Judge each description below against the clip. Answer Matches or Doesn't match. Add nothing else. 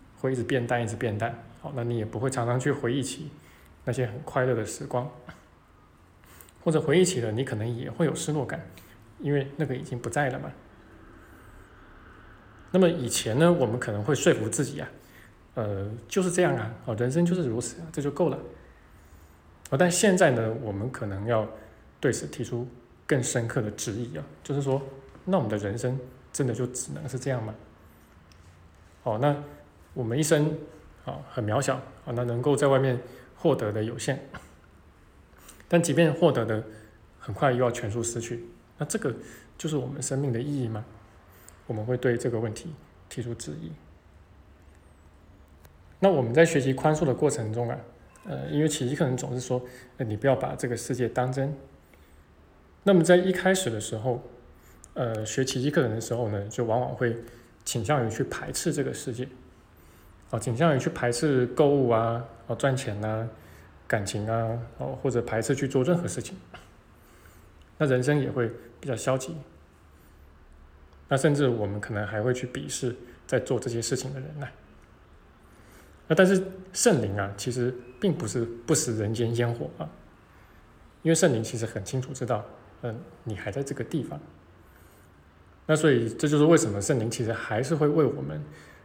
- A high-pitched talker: Doesn't match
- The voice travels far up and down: Doesn't match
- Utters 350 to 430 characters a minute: Doesn't match